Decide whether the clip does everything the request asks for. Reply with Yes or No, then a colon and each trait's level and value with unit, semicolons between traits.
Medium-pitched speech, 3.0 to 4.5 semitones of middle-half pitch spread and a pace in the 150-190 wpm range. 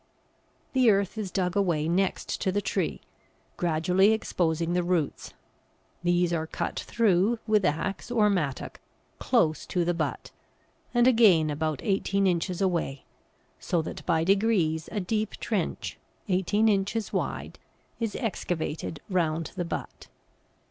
No: medium, 180 Hz; average, 3.7 semitones; slow, 135 wpm